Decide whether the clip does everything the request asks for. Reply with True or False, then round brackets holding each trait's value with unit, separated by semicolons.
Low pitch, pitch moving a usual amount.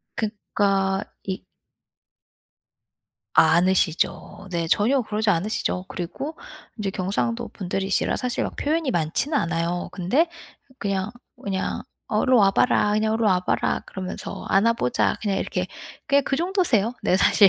False (195 Hz; 3.9 semitones)